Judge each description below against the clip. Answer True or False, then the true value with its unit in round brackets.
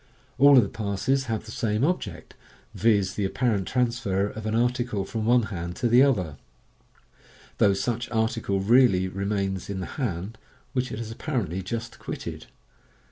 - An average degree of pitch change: True (3.8 semitones)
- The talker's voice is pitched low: True (110 Hz)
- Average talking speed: True (165 wpm)